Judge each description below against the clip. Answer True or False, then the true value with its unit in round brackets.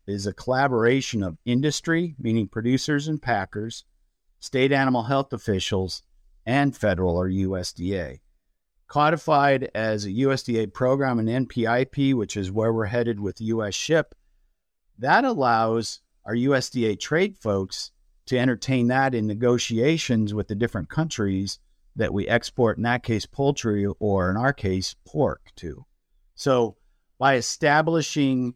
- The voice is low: True (115 Hz)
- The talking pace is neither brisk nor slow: False (130 wpm)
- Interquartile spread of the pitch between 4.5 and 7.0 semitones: True (5.0 semitones)